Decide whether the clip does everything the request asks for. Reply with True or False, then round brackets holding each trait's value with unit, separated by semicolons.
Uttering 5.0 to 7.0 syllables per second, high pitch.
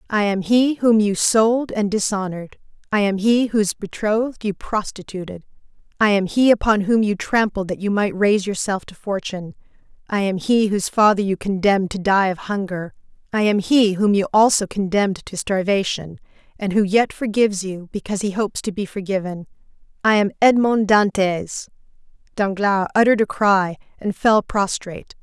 True (5.2 syllables/s; 200 Hz)